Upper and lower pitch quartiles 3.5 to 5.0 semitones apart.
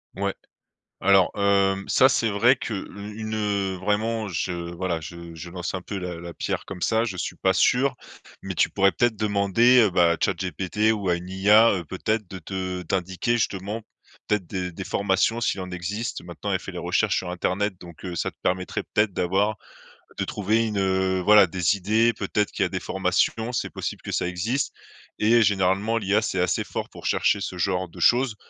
No: average, 2.9 semitones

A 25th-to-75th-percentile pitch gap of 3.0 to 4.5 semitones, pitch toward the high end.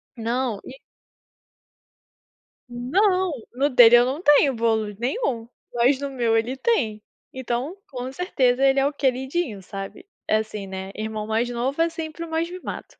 Yes: average, 4.2 semitones; very high, 255 Hz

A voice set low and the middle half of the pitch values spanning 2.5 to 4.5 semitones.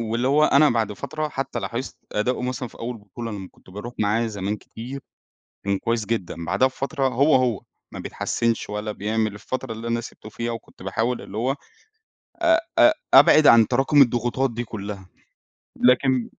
Yes: low, 115 Hz; average, 3.6 semitones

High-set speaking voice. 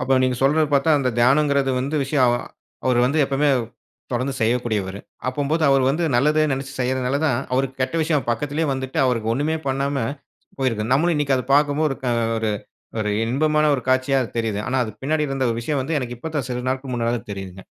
No: low, 130 Hz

